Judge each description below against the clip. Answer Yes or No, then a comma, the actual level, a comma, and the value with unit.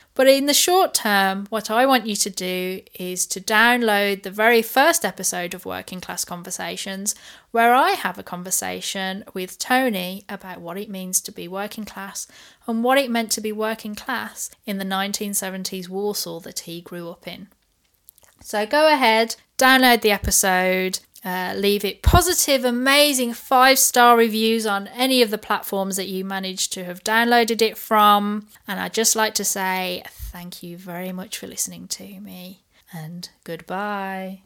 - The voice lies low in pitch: No, high, 200 Hz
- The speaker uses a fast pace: No, average, 170 wpm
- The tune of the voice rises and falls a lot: No, average, 3.4 semitones